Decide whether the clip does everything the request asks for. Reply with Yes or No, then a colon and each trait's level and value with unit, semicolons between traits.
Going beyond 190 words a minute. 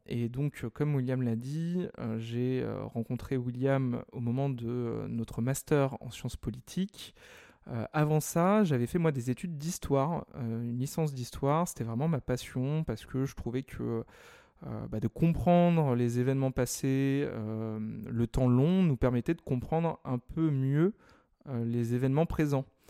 No: slow, 145 wpm